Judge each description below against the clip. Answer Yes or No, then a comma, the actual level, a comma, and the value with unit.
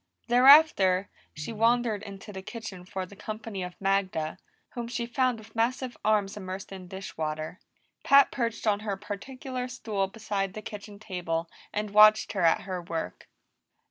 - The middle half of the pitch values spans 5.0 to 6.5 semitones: No, average, 3.5 semitones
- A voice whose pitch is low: No, high, 205 Hz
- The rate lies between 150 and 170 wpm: Yes, average, 160 wpm